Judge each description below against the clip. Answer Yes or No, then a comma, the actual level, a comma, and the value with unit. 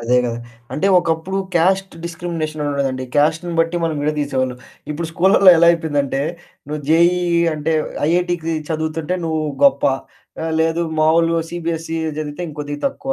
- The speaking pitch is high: No, medium, 160 Hz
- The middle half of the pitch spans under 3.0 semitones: Yes, narrow, 2.4 semitones